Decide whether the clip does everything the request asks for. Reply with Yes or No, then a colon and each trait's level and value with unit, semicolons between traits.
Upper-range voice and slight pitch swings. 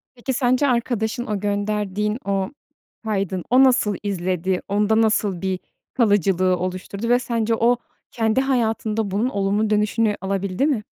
No: high, 210 Hz; average, 3.1 semitones